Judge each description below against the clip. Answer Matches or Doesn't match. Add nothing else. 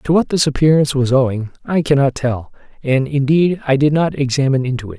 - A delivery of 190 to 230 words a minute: Matches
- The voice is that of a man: Matches